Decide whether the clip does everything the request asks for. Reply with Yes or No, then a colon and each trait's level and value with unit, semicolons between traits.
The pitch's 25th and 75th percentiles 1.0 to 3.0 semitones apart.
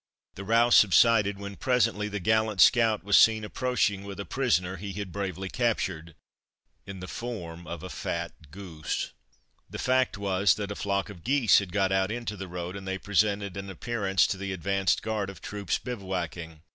Yes: narrow, 2.6 semitones